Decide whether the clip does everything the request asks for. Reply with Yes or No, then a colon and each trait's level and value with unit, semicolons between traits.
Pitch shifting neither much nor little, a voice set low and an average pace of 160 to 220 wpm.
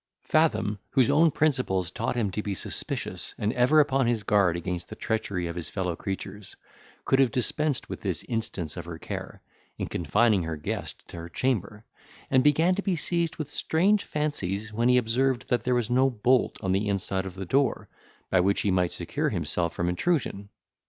No: wide, 5.9 semitones; low, 110 Hz; average, 195 wpm